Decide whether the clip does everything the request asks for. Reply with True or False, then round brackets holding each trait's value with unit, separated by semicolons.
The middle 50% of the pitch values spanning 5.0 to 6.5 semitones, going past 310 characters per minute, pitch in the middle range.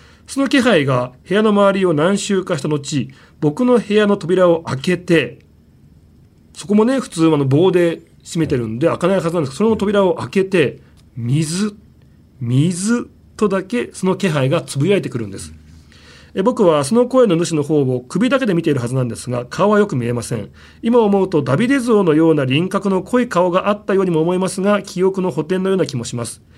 False (7.2 semitones; 365 characters per minute; 175 Hz)